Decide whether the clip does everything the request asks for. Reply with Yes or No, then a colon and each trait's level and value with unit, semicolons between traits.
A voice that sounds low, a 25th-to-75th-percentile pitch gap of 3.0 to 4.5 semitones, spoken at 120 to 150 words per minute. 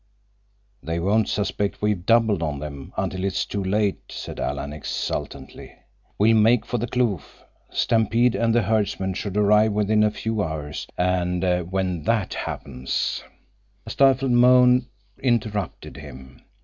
Yes: low, 105 Hz; average, 4.1 semitones; average, 140 wpm